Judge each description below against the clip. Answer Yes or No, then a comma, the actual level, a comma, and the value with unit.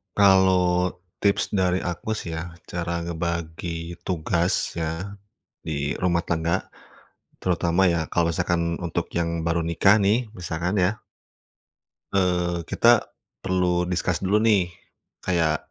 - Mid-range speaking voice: No, very low, 85 Hz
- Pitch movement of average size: No, narrow, 1.8 semitones